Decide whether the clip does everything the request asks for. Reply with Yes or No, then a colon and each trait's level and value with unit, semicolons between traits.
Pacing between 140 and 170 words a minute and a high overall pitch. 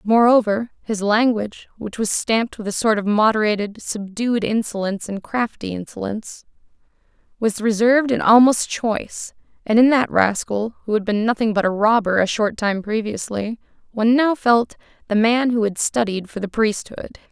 Yes: average, 165 wpm; high, 220 Hz